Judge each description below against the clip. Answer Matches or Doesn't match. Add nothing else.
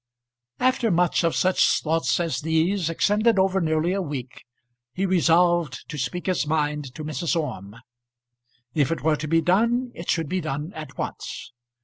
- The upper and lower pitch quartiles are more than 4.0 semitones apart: Doesn't match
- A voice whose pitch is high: Doesn't match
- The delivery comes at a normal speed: Matches